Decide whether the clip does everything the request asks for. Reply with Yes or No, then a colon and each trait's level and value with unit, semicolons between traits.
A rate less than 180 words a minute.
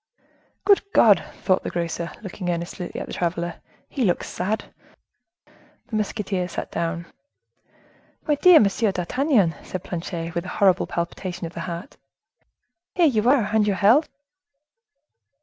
Yes: average, 140 wpm